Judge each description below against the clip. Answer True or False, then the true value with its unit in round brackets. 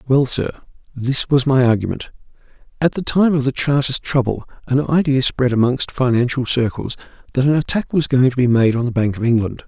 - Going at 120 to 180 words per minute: False (200 wpm)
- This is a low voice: True (130 Hz)